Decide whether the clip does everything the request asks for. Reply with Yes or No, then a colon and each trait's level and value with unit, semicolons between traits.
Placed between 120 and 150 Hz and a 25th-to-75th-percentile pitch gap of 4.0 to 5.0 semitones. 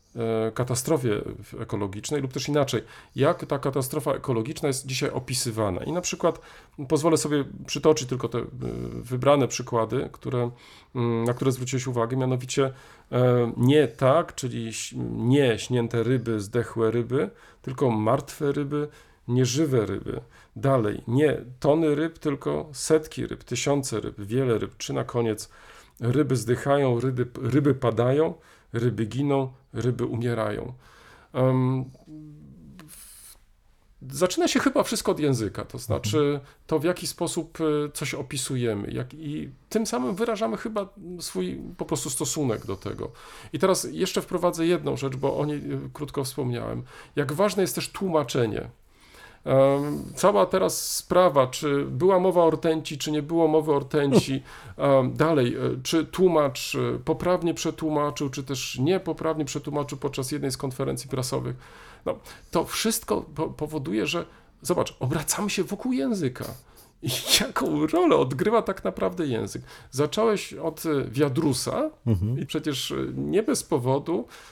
Yes: medium, 140 Hz; average, 4.4 semitones